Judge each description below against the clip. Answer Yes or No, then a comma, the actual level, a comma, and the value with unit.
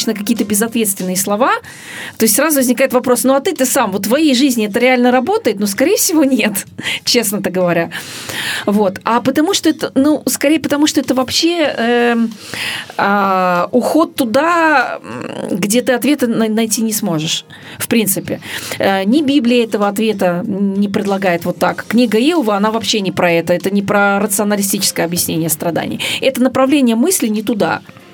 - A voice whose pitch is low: No, high, 230 Hz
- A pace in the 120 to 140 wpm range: No, average, 155 wpm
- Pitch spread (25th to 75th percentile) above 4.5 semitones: Yes, average, 5.0 semitones